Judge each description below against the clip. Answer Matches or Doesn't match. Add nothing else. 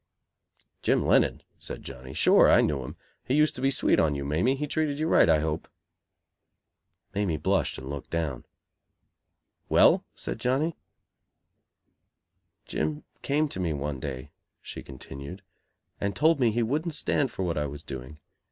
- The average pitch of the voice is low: Matches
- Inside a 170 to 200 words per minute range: Doesn't match